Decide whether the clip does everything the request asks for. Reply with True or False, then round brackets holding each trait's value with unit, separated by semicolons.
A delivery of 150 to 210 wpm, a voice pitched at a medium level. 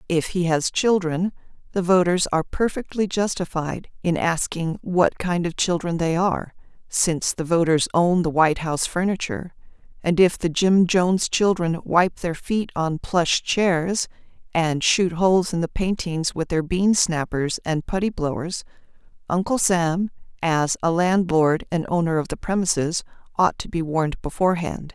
True (155 wpm; 175 Hz)